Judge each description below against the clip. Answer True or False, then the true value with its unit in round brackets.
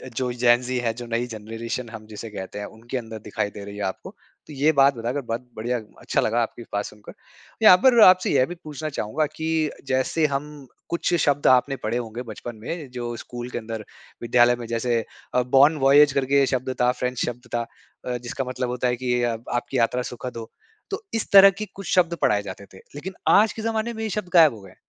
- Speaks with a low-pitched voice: True (125 Hz)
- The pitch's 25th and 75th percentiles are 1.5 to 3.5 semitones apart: False (3.9 semitones)